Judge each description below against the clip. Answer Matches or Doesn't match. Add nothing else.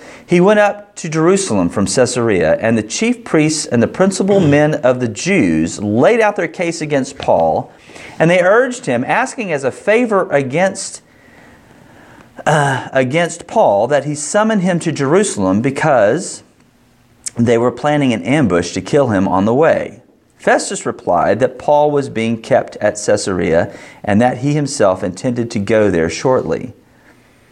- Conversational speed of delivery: Matches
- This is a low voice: Doesn't match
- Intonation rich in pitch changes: Matches